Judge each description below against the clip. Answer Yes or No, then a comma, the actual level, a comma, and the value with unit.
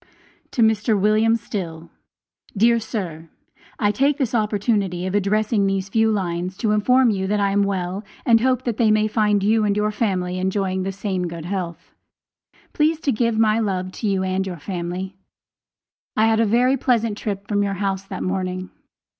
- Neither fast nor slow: Yes, average, 180 wpm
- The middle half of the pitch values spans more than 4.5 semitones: No, average, 2.8 semitones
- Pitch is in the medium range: No, high, 205 Hz